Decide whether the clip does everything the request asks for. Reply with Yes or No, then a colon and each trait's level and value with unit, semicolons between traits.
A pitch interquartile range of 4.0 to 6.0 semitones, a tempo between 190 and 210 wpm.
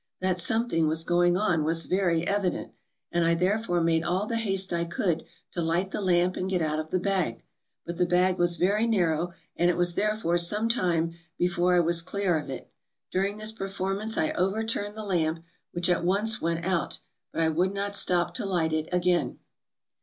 No: narrow, 2.6 semitones; average, 200 wpm